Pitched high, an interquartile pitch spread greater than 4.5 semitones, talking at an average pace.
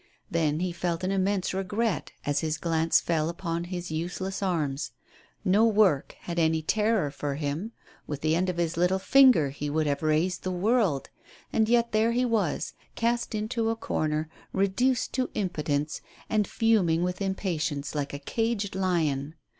No: medium, 180 Hz; average, 5.2 semitones; average, 170 wpm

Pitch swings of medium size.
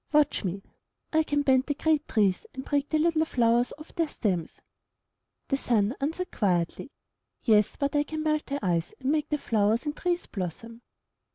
No: wide, 6.2 semitones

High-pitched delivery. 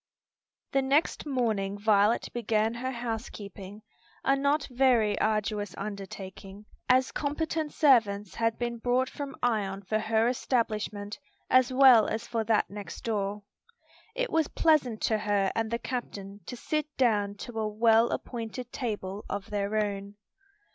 Yes: high, 225 Hz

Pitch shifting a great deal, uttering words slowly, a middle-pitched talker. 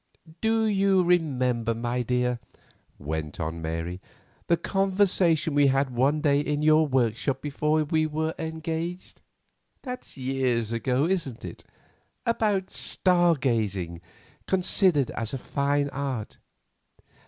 Yes: wide, 5.7 semitones; slow, 110 wpm; medium, 145 Hz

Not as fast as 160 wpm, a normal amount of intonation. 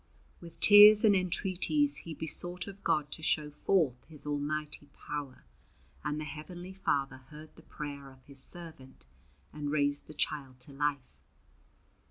Yes: average, 150 wpm; average, 3.6 semitones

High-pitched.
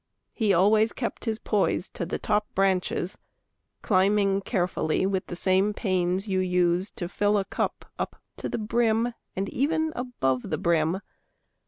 Yes: high, 195 Hz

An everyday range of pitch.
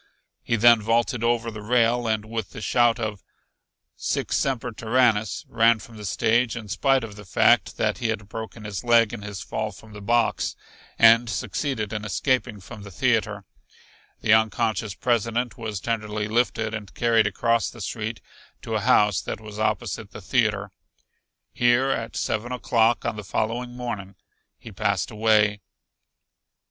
No: narrow, 2.0 semitones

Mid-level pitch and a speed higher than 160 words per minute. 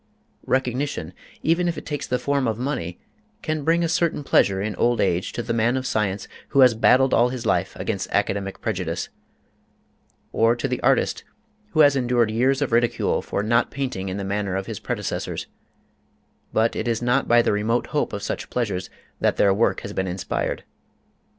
No: low, 120 Hz; average, 190 wpm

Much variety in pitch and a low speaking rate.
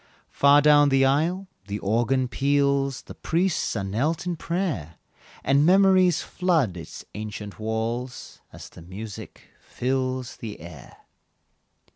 Yes: wide, 6.2 semitones; slow, 125 wpm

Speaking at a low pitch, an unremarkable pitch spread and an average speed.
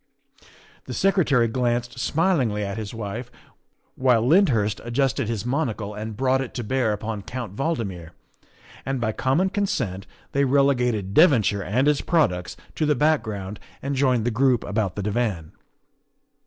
Yes: low, 120 Hz; average, 4.6 semitones; average, 145 wpm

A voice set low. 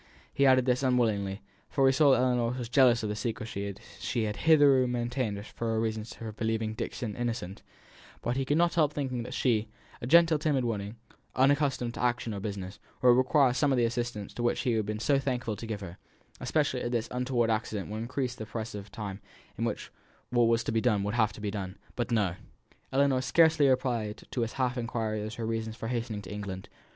Yes: low, 120 Hz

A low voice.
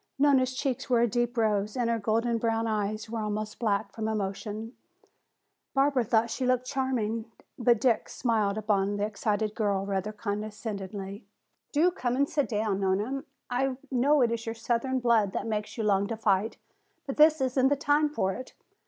No: high, 225 Hz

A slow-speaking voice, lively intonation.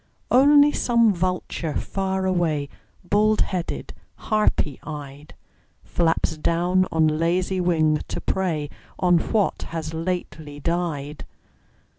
No: slow, 105 wpm; average, 3.4 semitones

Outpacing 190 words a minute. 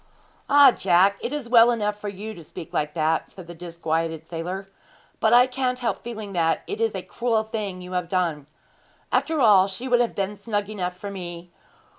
Yes: average, 200 wpm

